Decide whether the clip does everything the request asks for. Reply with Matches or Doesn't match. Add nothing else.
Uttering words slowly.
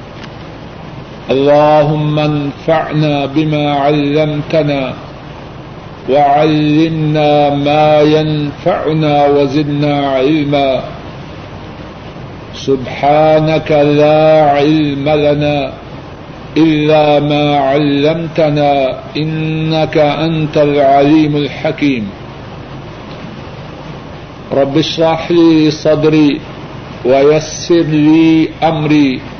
Matches